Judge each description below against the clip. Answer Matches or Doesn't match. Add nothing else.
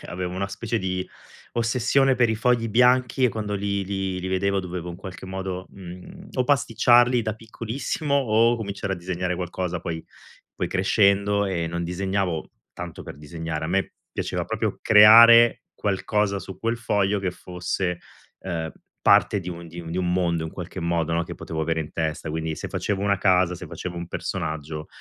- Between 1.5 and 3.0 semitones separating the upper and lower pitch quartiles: Doesn't match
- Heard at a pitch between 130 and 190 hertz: Doesn't match